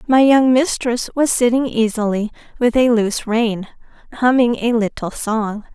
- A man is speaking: No, female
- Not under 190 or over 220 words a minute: No, average, 145 wpm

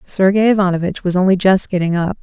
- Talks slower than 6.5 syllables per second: Yes, 6.3 syllables/s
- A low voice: No, medium, 185 Hz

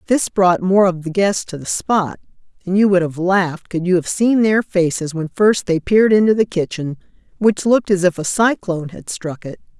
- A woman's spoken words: Yes, female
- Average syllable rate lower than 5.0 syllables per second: No, 5.2 syllables/s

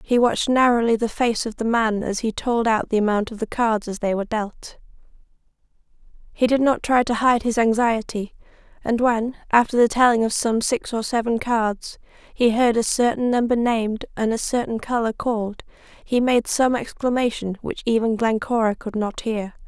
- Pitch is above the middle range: Yes, high, 230 Hz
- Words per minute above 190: No, average, 185 wpm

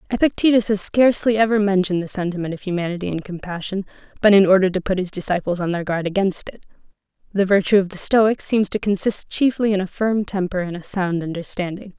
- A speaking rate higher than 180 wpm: Yes, average, 200 wpm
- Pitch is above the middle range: Yes, high, 195 Hz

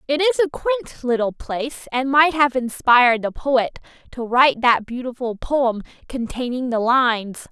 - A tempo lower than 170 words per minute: Yes, average, 160 wpm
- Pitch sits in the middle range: No, very high, 255 Hz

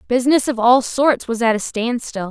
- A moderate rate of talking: No, fast, 210 wpm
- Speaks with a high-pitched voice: Yes, high, 240 Hz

